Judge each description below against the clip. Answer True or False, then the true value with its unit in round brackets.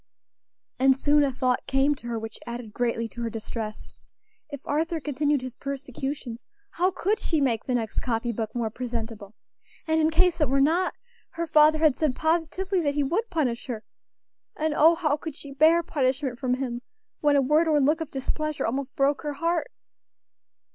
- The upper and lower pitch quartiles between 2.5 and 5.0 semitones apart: True (4.2 semitones)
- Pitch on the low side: False (280 Hz)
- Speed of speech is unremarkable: True (185 wpm)